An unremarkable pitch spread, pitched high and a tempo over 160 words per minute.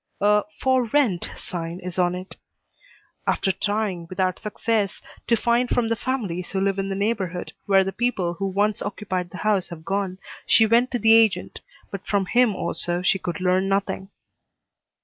Yes: average, 3.2 semitones; high, 195 Hz; average, 175 wpm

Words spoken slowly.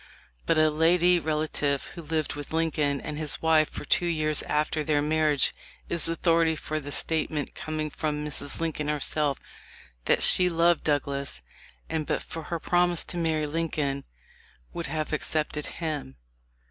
No: average, 155 wpm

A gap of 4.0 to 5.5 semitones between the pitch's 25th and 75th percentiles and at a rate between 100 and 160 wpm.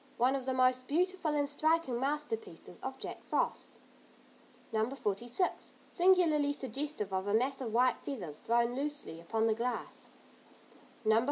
Yes: average, 4.5 semitones; average, 145 wpm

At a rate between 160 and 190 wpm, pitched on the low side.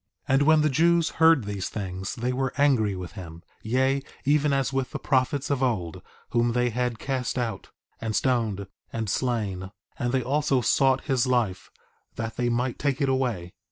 Yes: average, 185 wpm; low, 125 Hz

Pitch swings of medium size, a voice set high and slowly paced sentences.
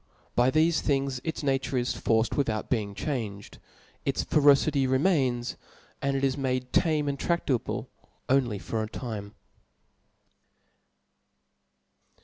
No: average, 3.0 semitones; low, 130 Hz; slow, 125 wpm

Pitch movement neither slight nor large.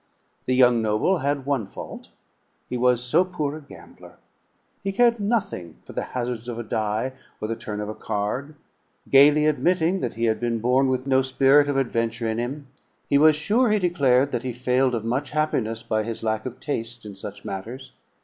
Yes: average, 4.3 semitones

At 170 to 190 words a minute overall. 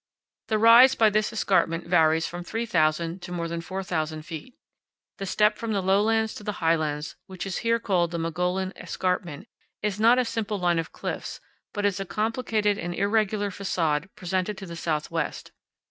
Yes: average, 175 wpm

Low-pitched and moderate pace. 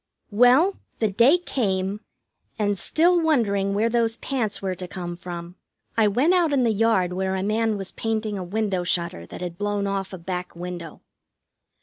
No: high, 205 Hz; average, 180 wpm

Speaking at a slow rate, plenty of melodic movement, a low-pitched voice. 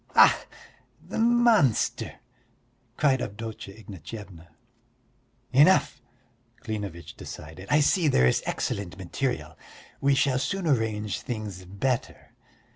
Yes: slow, 100 wpm; wide, 6.6 semitones; low, 110 Hz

